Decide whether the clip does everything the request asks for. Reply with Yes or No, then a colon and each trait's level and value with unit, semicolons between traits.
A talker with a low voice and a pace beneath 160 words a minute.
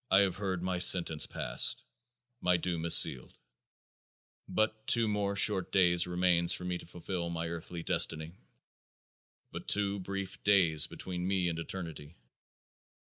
Yes: very low, 90 Hz; average, 140 wpm